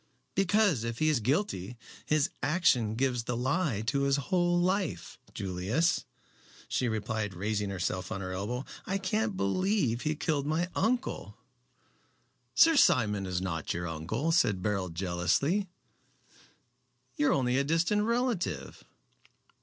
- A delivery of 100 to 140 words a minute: Yes, slow, 135 wpm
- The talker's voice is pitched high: No, low, 130 Hz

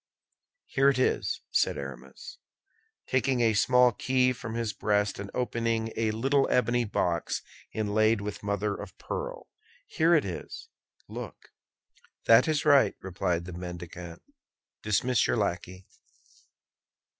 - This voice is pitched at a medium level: No, low, 110 Hz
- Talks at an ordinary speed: No, slow, 125 wpm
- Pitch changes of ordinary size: Yes, average, 4.3 semitones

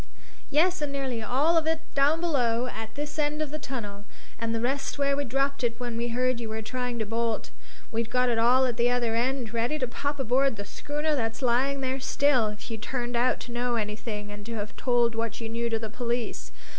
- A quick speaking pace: Yes, fast, 230 wpm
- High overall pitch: Yes, high, 245 Hz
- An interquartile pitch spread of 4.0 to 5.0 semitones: No, average, 3.3 semitones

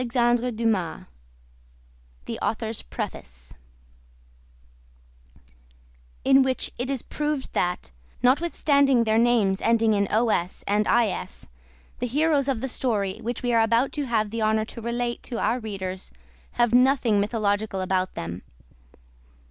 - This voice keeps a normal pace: No, slow, 125 wpm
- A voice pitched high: Yes, high, 225 Hz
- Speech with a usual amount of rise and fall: Yes, average, 4.5 semitones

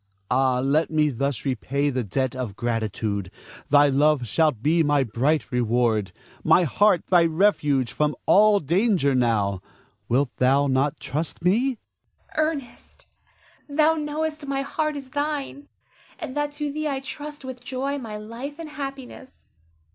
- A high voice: No, medium, 160 Hz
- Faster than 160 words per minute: No, average, 145 wpm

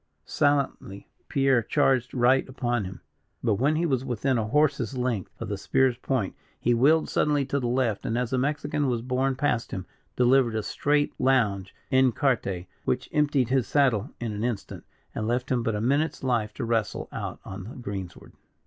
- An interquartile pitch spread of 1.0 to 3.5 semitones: Yes, average, 3.2 semitones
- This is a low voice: Yes, low, 125 Hz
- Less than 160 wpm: No, average, 185 wpm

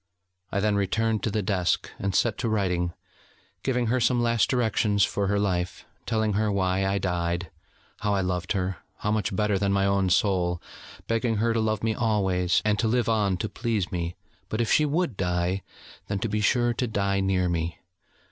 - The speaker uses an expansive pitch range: No, average, 3.3 semitones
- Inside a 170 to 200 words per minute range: Yes, average, 195 wpm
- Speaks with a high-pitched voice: No, low, 100 Hz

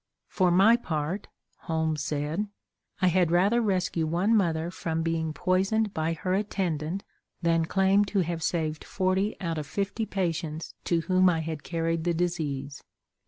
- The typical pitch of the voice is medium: Yes, medium, 170 Hz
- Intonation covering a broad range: No, average, 3.0 semitones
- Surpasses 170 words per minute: No, average, 155 wpm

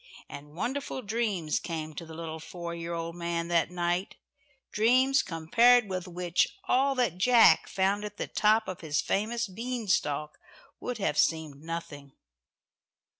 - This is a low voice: No, medium, 180 Hz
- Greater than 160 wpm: No, average, 150 wpm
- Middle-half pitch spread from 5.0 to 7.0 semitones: Yes, wide, 5.6 semitones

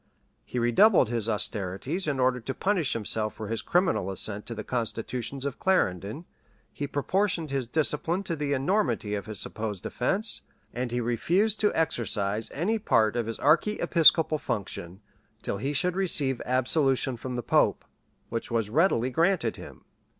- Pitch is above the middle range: No, low, 130 Hz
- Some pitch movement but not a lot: No, wide, 6.7 semitones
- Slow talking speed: No, average, 155 wpm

